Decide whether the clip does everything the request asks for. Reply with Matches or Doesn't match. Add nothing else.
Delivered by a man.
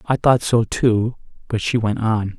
Matches